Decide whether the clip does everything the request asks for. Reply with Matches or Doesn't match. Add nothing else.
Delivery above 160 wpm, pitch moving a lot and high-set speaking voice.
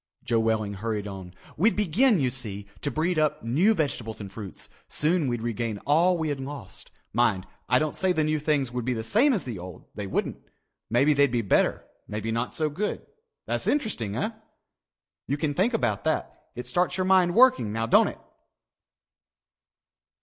Doesn't match